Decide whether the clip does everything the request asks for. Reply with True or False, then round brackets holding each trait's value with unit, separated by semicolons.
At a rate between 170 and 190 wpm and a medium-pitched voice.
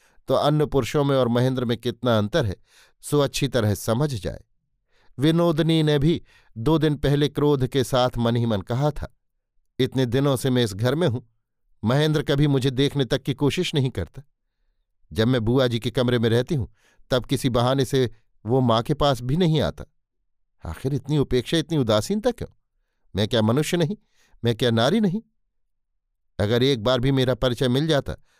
False (185 wpm; 130 Hz)